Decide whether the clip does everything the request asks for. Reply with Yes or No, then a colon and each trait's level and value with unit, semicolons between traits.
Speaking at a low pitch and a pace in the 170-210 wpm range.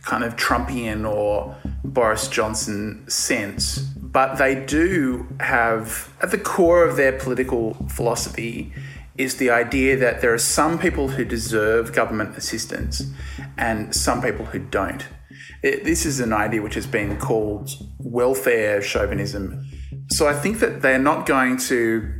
No: low, 115 Hz; average, 145 wpm